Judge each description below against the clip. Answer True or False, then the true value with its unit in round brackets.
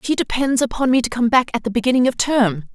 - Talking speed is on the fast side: True (265 wpm)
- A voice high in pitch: True (245 Hz)